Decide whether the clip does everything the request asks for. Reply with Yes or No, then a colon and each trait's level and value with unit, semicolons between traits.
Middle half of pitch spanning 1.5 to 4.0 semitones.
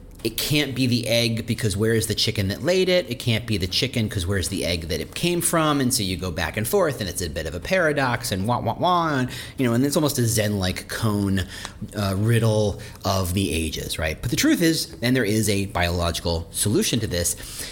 No: average, 4.5 semitones